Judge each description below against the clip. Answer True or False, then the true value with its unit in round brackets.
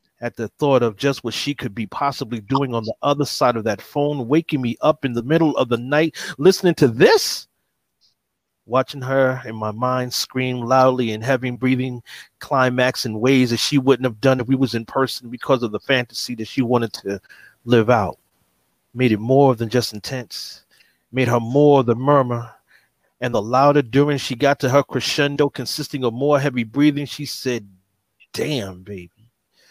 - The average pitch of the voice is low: True (130 Hz)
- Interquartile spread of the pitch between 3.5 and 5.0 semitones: False (3.1 semitones)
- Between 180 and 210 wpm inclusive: True (190 wpm)